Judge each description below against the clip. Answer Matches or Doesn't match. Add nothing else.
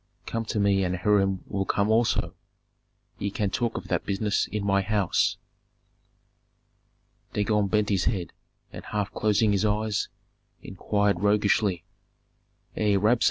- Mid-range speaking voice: Doesn't match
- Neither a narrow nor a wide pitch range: Doesn't match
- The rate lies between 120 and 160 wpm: Matches